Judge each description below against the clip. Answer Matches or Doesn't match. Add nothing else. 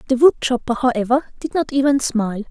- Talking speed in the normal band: Matches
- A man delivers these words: Doesn't match